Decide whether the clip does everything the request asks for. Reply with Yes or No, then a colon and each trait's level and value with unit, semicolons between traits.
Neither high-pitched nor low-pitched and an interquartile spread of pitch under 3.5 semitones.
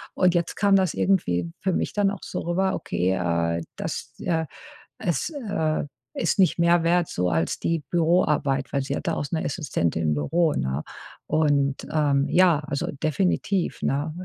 No: medium, 160 Hz; average, 4.3 semitones